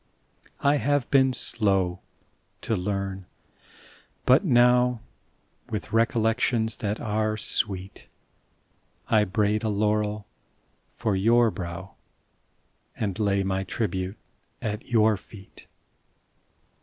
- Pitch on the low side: Yes, low, 105 Hz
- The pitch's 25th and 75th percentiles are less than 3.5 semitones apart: Yes, average, 2.8 semitones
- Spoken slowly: Yes, slow, 100 wpm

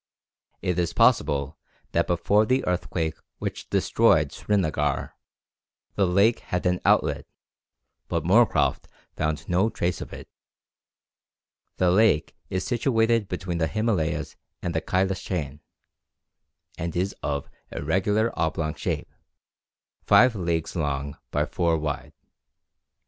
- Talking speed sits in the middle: No, slow, 115 wpm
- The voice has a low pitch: Yes, very low, 90 Hz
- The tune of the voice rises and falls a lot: No, average, 4.3 semitones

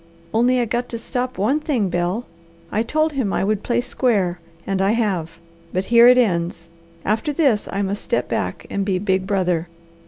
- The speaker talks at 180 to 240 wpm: Yes, average, 190 wpm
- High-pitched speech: Yes, high, 210 Hz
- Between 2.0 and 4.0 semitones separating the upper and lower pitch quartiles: No, average, 4.6 semitones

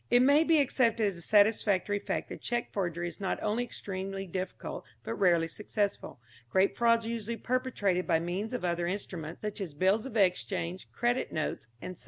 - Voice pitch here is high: Yes, high, 200 Hz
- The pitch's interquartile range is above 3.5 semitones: Yes, average, 4.3 semitones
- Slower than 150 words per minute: No, average, 185 wpm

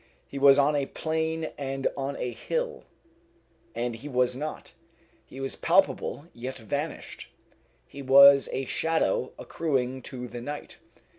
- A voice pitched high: No, low, 135 Hz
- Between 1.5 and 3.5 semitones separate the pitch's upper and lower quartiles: Yes, narrow, 2.6 semitones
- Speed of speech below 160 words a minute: Yes, average, 140 wpm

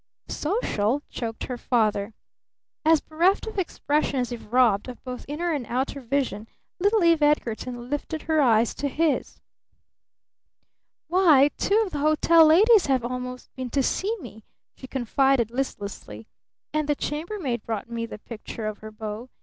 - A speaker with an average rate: Yes, average, 155 wpm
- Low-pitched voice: No, very high, 265 Hz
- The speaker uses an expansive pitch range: No, average, 5.0 semitones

